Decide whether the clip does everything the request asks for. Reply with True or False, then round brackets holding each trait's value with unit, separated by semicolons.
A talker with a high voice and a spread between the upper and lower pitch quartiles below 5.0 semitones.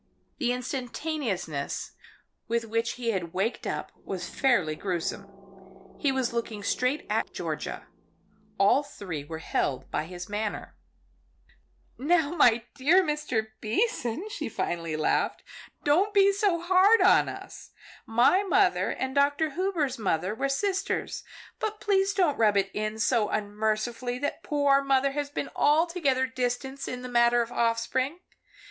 False (250 Hz; 5.6 semitones)